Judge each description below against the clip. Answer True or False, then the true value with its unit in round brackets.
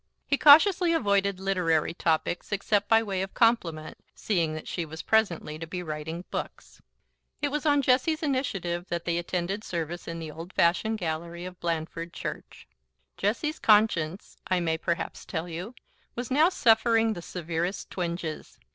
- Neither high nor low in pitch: True (180 Hz)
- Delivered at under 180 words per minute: True (155 wpm)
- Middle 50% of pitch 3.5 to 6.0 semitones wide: True (5.0 semitones)